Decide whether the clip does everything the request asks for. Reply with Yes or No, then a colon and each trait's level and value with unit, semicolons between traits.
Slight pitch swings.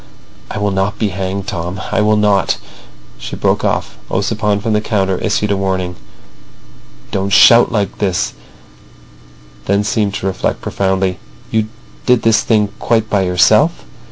Yes: narrow, 1.8 semitones